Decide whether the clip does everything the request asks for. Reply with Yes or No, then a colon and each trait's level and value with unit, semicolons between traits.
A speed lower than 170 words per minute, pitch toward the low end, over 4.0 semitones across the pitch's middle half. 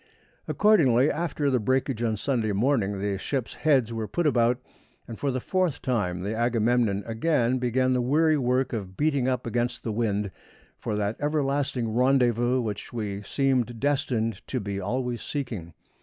No: average, 160 wpm; low, 120 Hz; average, 3.6 semitones